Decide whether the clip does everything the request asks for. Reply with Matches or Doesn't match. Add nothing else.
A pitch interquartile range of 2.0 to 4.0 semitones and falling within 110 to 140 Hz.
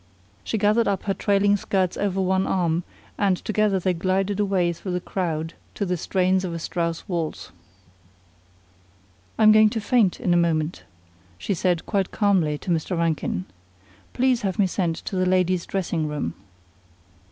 Doesn't match